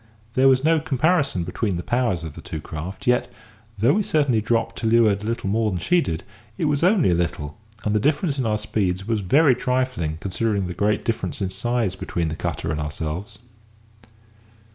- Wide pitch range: Yes, wide, 6.3 semitones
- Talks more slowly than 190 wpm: No, average, 200 wpm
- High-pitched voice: No, low, 110 Hz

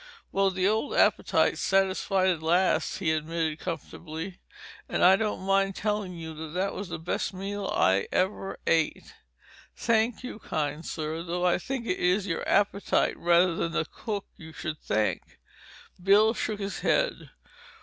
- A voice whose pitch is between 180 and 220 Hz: Yes, medium, 185 Hz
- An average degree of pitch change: Yes, average, 3.4 semitones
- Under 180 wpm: Yes, average, 155 wpm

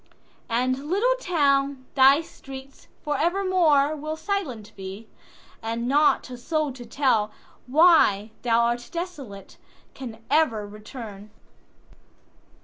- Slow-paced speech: Yes, slow, 100 wpm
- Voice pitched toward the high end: Yes, very high, 270 Hz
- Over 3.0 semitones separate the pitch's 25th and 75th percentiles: Yes, average, 5.3 semitones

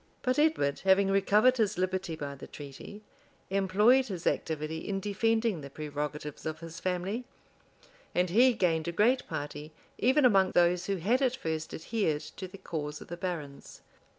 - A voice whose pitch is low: No, medium, 185 Hz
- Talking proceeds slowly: No, average, 165 wpm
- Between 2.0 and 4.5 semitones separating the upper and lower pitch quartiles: No, average, 5.2 semitones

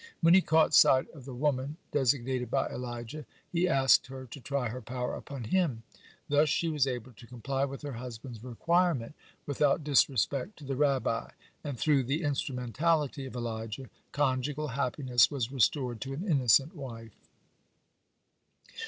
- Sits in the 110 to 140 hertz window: Yes, low, 135 Hz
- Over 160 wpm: No, average, 155 wpm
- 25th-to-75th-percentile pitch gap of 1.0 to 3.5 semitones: Yes, average, 3.0 semitones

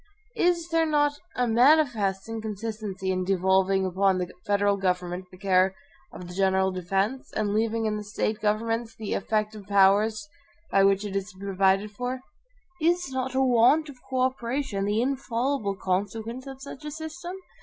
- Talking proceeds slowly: No, average, 165 wpm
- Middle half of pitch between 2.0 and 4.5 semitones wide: No, average, 5.0 semitones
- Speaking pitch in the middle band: No, high, 215 Hz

